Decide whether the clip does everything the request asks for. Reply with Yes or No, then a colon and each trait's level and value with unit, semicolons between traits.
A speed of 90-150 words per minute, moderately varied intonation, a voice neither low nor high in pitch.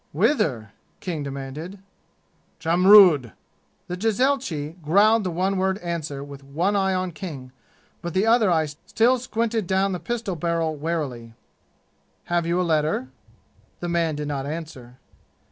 Yes: average, 140 wpm; average, 4.5 semitones; medium, 170 Hz